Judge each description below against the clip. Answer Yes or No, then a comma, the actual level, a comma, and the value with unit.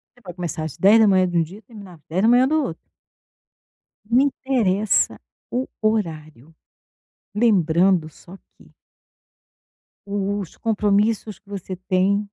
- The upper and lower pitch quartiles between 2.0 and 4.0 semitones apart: Yes, average, 3.6 semitones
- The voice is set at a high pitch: Yes, high, 200 Hz